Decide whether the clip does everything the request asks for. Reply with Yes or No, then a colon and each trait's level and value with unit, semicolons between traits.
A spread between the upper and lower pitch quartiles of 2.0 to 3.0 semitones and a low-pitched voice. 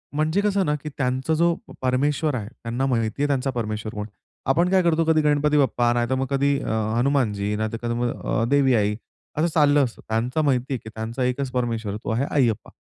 No: average, 4.1 semitones; low, 130 Hz